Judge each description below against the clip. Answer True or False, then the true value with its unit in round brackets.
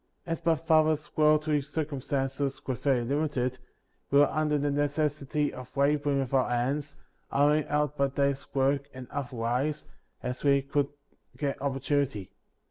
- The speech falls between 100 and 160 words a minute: True (150 wpm)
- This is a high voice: False (140 Hz)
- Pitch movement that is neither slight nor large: False (1.8 semitones)